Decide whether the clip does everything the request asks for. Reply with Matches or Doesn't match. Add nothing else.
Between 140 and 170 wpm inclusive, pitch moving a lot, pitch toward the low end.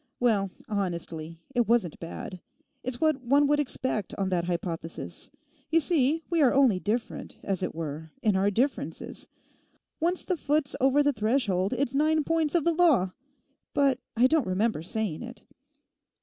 Doesn't match